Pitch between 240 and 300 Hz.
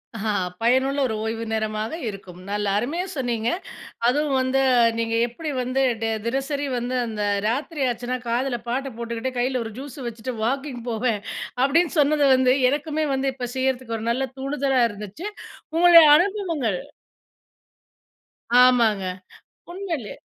Yes: very high, 255 Hz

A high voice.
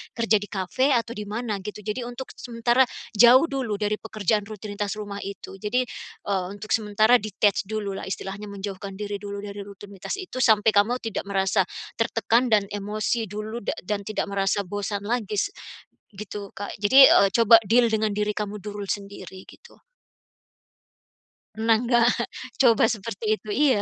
Yes: high, 210 Hz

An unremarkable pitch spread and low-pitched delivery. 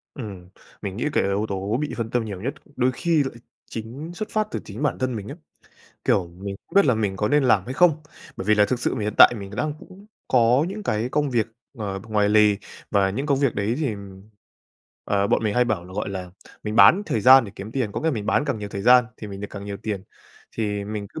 Yes: average, 4.7 semitones; low, 110 Hz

